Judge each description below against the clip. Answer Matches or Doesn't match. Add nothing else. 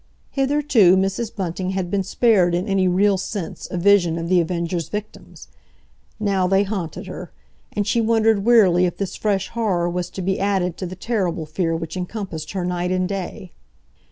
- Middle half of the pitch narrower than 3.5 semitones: Matches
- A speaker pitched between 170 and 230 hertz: Matches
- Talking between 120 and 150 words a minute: Doesn't match